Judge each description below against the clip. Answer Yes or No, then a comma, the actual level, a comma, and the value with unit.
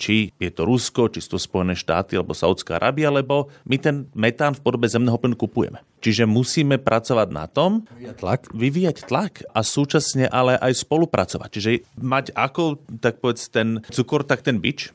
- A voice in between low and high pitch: No, low, 125 Hz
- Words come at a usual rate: No, fast, 175 wpm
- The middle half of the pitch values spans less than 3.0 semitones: No, average, 4.0 semitones